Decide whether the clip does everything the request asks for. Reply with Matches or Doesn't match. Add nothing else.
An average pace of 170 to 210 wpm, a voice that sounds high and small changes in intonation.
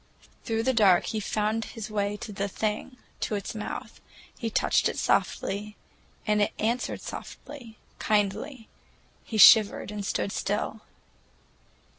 Doesn't match